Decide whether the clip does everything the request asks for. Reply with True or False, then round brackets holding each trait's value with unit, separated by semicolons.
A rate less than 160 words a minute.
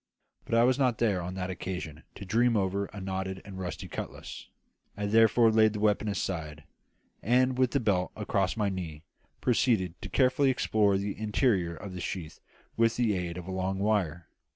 False (185 wpm)